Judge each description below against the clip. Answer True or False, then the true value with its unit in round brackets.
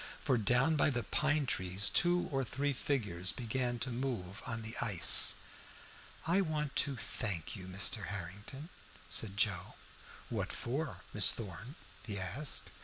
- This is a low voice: True (120 Hz)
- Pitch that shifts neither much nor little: False (5.9 semitones)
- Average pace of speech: True (145 wpm)